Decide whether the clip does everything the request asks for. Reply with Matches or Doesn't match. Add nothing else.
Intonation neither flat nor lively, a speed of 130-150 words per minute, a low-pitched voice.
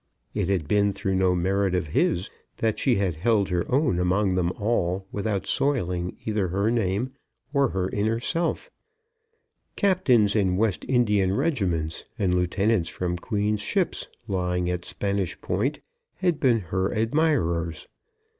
Matches